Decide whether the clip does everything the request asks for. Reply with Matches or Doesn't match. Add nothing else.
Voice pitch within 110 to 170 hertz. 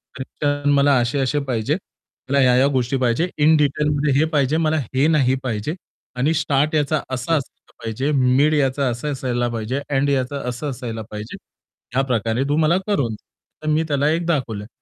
Matches